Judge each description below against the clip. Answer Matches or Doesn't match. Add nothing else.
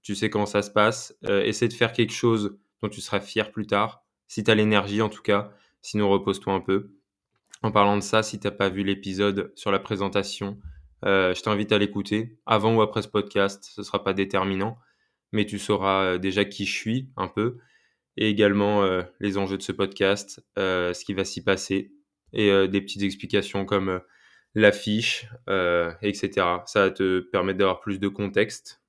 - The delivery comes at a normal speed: Matches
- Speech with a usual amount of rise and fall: Doesn't match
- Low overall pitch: Matches